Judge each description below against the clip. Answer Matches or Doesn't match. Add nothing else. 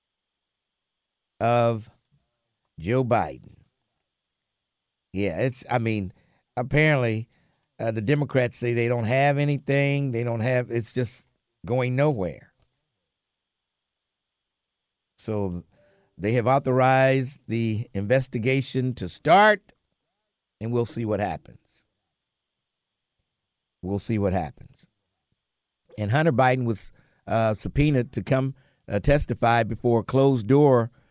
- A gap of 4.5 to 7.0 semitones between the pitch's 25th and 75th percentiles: Doesn't match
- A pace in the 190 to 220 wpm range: Doesn't match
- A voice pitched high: Doesn't match